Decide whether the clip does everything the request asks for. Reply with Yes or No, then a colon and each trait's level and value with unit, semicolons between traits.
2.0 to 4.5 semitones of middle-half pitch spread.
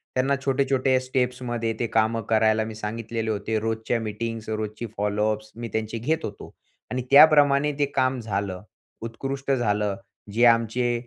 Yes: average, 2.9 semitones